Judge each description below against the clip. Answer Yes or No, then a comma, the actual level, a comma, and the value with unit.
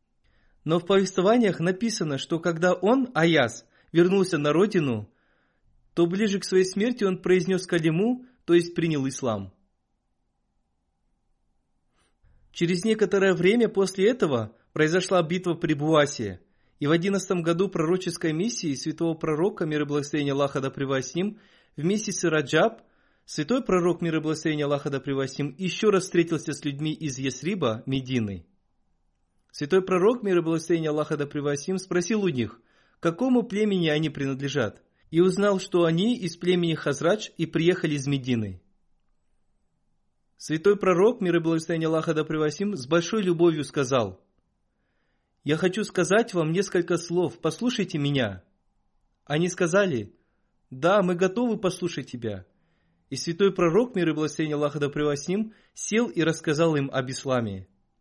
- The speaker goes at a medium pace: Yes, average, 140 wpm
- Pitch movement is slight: No, average, 4.6 semitones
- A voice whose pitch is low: No, medium, 170 Hz